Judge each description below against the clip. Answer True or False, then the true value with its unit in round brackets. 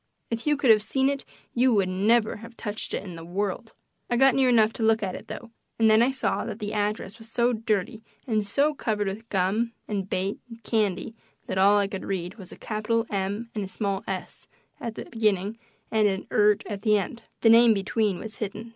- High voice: True (215 Hz)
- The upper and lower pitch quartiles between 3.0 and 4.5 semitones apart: False (2.6 semitones)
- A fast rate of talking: True (225 wpm)